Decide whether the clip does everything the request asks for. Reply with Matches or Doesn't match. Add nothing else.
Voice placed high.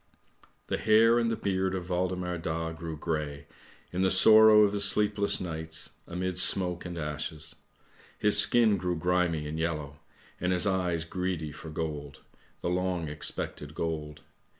Doesn't match